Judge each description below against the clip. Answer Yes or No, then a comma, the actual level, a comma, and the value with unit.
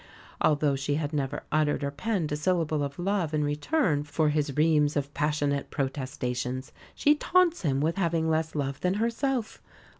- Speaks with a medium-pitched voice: Yes, medium, 150 Hz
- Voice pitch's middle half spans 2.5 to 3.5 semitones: Yes, average, 3.0 semitones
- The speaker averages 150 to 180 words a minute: Yes, average, 170 wpm